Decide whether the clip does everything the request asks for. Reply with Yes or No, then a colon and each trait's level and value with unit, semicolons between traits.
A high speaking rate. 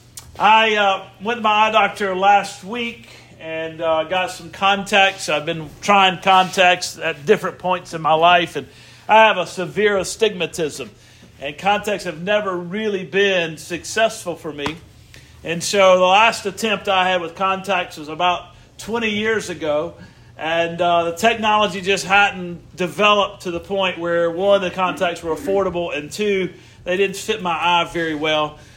No: average, 165 wpm